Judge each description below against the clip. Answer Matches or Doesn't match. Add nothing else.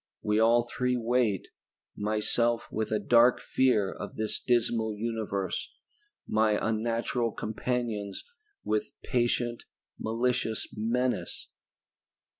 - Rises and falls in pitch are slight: Matches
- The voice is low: Matches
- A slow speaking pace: Matches